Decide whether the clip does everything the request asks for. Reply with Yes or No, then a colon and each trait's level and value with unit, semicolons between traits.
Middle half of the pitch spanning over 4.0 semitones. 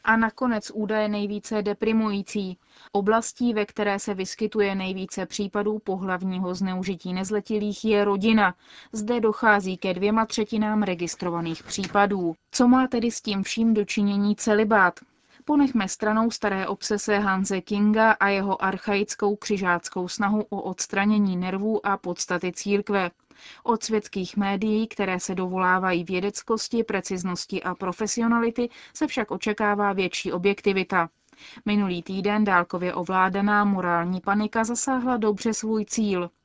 No: narrow, 2.5 semitones